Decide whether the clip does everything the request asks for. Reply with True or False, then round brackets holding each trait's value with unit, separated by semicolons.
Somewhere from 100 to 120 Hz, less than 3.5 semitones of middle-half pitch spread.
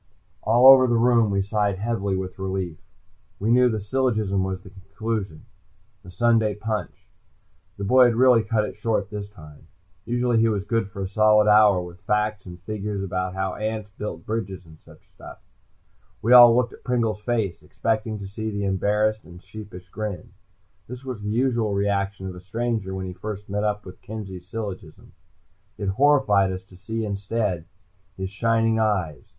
True (105 Hz; 2.8 semitones)